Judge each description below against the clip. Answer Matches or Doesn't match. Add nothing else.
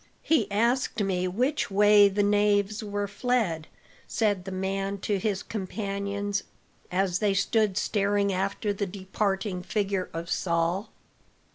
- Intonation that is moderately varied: Doesn't match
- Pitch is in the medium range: Doesn't match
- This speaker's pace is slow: Matches